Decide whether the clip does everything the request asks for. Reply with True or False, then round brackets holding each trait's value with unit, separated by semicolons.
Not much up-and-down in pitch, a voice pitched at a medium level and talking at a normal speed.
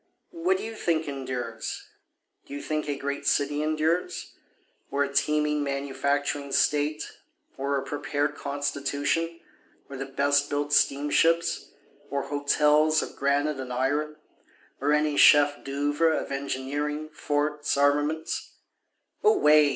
False (1.4 semitones; 145 Hz; 125 wpm)